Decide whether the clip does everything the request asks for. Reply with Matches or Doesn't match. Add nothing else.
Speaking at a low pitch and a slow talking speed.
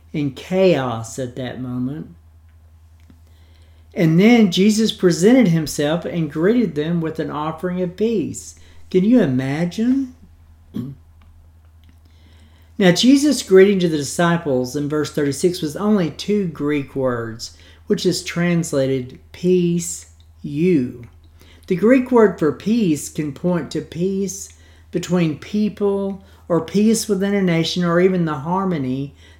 Doesn't match